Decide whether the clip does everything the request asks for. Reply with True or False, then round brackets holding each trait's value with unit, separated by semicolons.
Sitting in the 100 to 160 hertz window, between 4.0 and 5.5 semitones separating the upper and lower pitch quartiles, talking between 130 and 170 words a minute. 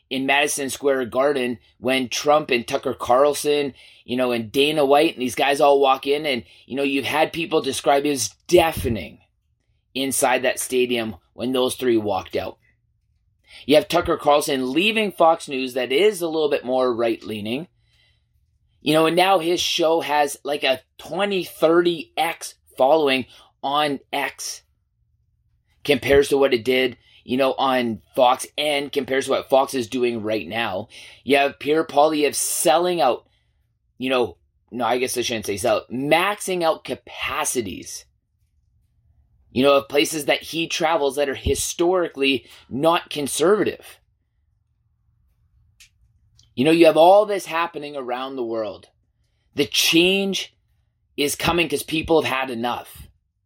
True (135 Hz; 4.7 semitones; 150 wpm)